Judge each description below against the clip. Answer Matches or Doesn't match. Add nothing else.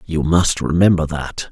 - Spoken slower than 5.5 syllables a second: Matches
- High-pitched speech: Doesn't match